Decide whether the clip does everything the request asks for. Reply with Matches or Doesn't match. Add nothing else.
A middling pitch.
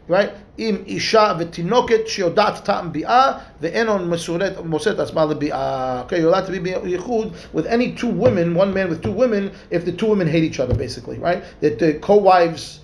Matches